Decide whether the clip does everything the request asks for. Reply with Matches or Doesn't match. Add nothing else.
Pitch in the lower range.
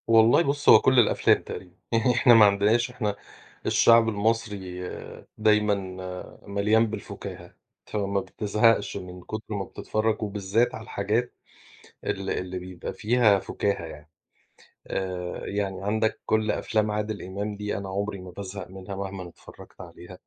Matches